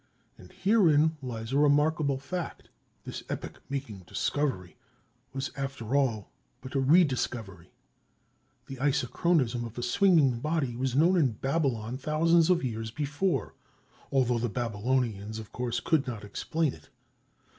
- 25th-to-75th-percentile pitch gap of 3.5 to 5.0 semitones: Yes, average, 4.5 semitones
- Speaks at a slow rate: Yes, slow, 130 wpm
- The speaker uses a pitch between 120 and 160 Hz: Yes, low, 135 Hz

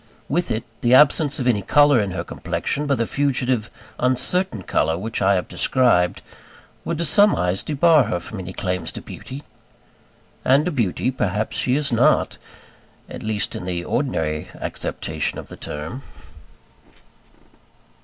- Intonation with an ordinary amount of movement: No, wide, 7.2 semitones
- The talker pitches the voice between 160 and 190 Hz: No, low, 120 Hz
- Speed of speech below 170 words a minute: Yes, average, 155 wpm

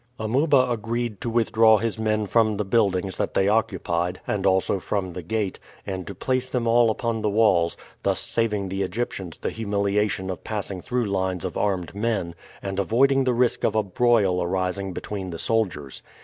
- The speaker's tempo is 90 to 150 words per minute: No, average, 180 wpm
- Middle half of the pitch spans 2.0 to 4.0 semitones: Yes, average, 3.3 semitones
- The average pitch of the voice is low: Yes, low, 105 Hz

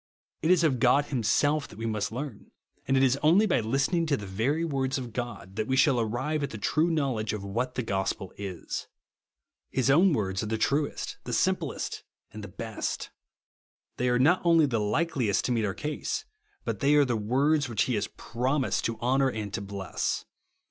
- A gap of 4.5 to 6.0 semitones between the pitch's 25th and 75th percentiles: Yes, average, 5.1 semitones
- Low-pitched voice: Yes, low, 125 Hz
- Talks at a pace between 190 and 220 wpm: Yes, average, 200 wpm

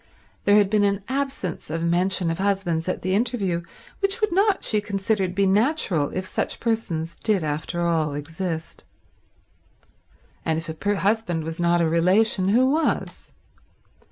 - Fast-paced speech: No, average, 155 wpm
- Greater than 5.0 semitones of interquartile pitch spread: No, average, 4.4 semitones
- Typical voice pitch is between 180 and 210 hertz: Yes, high, 190 Hz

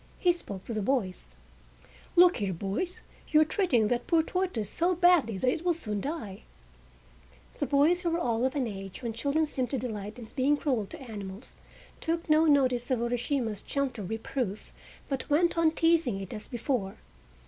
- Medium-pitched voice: No, very high, 255 Hz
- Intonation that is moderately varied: No, wide, 6.6 semitones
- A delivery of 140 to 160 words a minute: No, average, 180 wpm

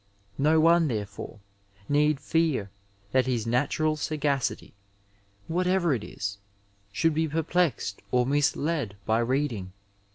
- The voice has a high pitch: No, medium, 145 Hz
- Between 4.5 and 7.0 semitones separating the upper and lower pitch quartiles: Yes, average, 5.2 semitones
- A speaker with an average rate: No, slow, 110 wpm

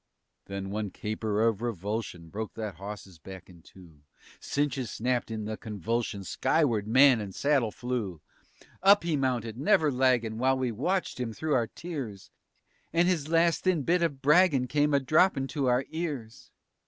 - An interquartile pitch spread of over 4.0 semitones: Yes, wide, 5.5 semitones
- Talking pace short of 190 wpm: Yes, average, 165 wpm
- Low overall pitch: Yes, low, 125 Hz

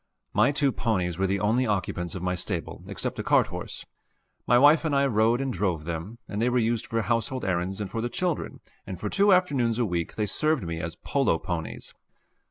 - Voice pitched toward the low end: Yes, low, 110 Hz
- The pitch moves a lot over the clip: Yes, wide, 5.9 semitones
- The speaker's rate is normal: No, fast, 215 wpm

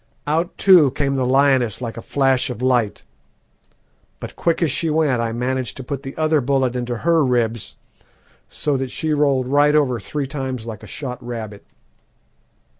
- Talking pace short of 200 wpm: Yes, average, 175 wpm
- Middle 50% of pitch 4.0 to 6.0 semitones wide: No, average, 3.1 semitones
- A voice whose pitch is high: No, low, 130 Hz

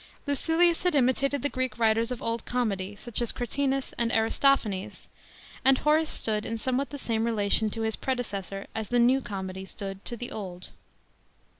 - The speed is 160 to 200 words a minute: Yes, average, 175 wpm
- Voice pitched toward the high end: Yes, high, 235 Hz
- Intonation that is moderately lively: Yes, average, 4.0 semitones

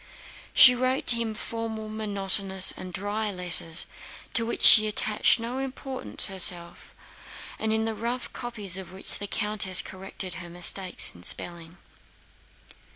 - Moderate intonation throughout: Yes, average, 3.5 semitones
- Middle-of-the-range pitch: No, high, 205 Hz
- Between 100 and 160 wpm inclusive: Yes, average, 140 wpm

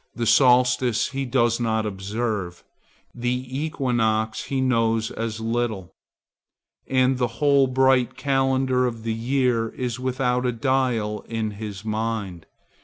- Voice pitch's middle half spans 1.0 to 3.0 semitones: Yes, narrow, 2.6 semitones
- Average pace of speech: No, slow, 125 wpm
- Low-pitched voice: Yes, low, 120 Hz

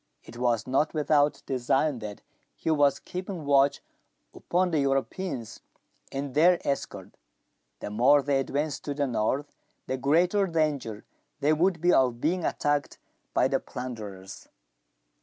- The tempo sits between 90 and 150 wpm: Yes, average, 140 wpm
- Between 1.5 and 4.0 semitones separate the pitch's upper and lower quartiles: Yes, average, 3.6 semitones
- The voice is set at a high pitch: No, medium, 140 Hz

